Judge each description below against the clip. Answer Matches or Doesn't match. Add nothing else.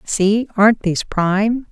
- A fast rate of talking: Doesn't match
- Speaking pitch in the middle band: Doesn't match